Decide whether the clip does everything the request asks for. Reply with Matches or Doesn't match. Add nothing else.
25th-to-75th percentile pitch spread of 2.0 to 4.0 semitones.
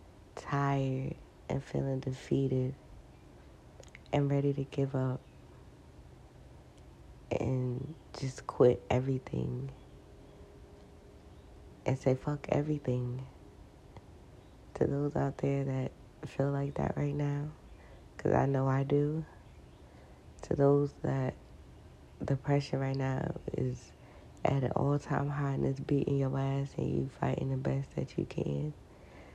Matches